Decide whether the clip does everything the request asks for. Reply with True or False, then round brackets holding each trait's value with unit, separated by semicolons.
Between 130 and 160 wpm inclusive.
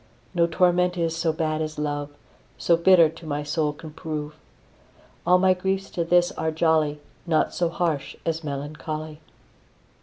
True (155 wpm)